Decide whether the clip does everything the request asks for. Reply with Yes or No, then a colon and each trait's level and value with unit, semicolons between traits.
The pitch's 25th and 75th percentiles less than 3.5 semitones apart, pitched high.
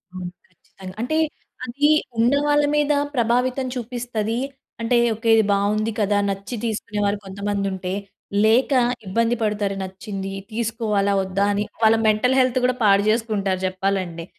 Yes: average, 3.1 semitones; high, 215 Hz